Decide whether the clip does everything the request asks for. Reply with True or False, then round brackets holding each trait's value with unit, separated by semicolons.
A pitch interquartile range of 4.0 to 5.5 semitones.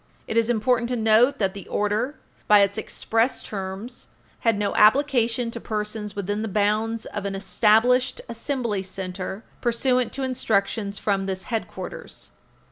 False (2.8 semitones)